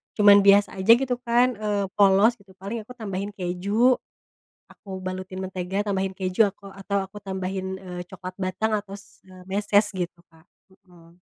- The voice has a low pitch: No, high, 195 Hz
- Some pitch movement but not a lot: No, narrow, 1.8 semitones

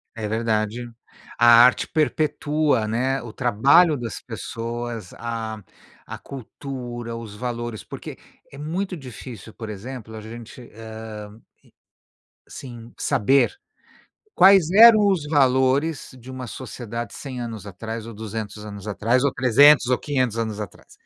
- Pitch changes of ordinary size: Yes, average, 3.5 semitones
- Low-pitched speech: Yes, low, 120 Hz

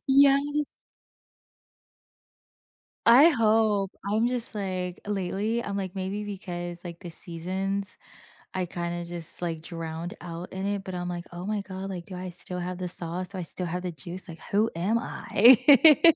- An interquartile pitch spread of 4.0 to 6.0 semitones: No, average, 3.2 semitones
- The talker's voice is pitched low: No, medium, 185 Hz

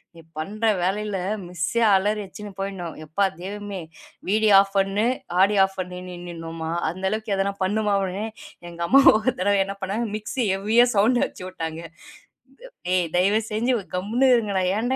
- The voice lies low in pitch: No, high, 200 Hz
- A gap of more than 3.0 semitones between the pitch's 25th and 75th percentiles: No, average, 2.7 semitones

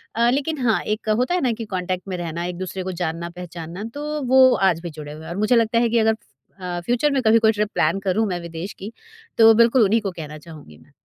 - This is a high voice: Yes, high, 195 Hz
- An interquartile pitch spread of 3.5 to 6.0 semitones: Yes, average, 5.2 semitones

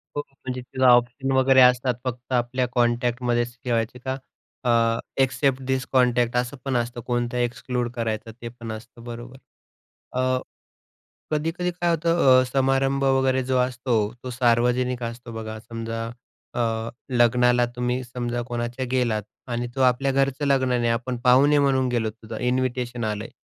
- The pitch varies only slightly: Yes, narrow, 1.7 semitones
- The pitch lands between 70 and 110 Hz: No, low, 125 Hz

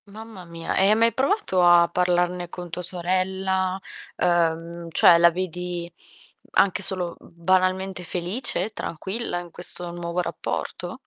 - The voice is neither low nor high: Yes, medium, 180 Hz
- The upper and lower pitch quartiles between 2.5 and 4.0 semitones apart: No, narrow, 1.7 semitones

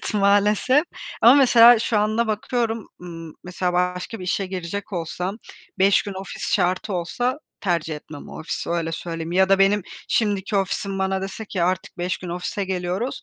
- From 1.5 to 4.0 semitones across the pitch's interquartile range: Yes, average, 2.9 semitones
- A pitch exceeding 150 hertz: Yes, high, 190 Hz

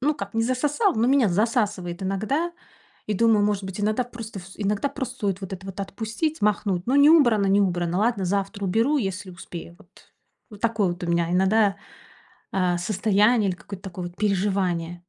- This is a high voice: Yes, high, 200 Hz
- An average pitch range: Yes, average, 3.5 semitones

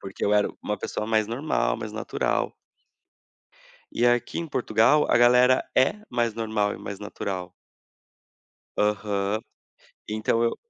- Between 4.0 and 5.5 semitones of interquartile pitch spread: No, average, 2.8 semitones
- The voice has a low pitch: Yes, low, 110 Hz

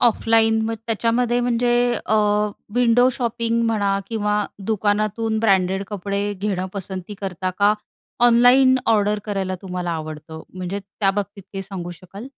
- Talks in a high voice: Yes, high, 205 Hz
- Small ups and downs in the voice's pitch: No, average, 3.0 semitones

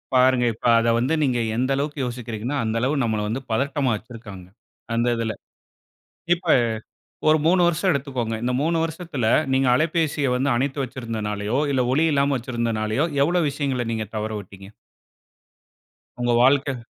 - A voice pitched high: No, low, 130 Hz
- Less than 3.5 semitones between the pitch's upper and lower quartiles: No, average, 3.8 semitones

